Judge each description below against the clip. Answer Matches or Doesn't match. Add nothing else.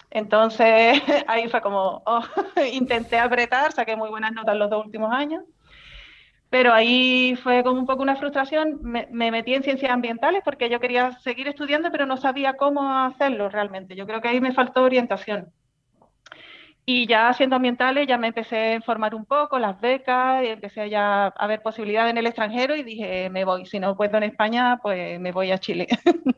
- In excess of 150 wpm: Matches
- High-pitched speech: Matches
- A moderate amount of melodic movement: Matches